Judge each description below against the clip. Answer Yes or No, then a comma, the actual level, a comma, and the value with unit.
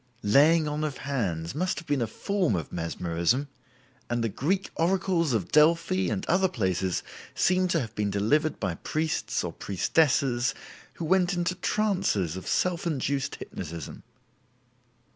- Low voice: No, medium, 145 Hz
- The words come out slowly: No, average, 145 wpm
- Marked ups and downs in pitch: Yes, wide, 9.0 semitones